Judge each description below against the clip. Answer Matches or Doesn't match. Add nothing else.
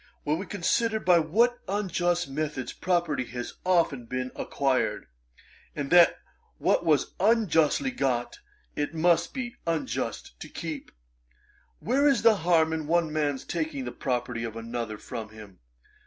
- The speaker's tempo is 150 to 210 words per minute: Doesn't match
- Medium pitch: Matches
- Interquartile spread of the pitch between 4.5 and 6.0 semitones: Matches